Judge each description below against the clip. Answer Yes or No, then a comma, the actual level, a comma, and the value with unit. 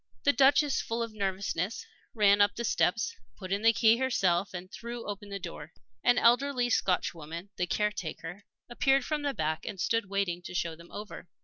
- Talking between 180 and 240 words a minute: Yes, average, 185 wpm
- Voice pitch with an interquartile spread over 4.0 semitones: Yes, average, 4.7 semitones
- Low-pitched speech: No, high, 205 Hz